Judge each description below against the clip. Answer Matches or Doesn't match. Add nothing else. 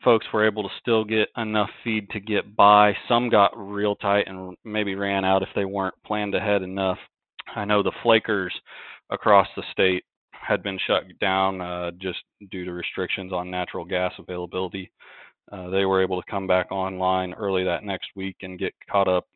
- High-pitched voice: Doesn't match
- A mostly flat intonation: Matches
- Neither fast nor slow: Matches